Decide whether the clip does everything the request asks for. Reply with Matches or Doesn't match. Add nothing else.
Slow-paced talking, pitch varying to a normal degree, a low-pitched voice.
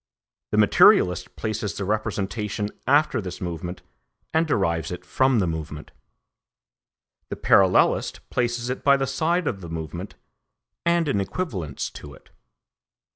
Doesn't match